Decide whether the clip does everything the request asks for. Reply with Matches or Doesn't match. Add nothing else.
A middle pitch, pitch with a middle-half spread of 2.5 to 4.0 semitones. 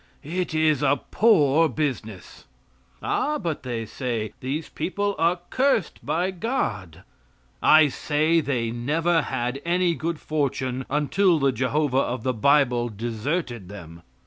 Doesn't match